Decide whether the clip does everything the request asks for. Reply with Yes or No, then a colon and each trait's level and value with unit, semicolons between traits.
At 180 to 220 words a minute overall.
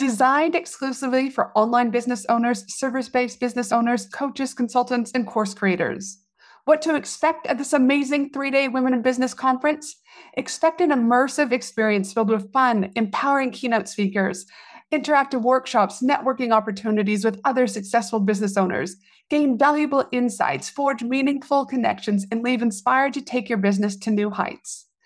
No: average, 150 wpm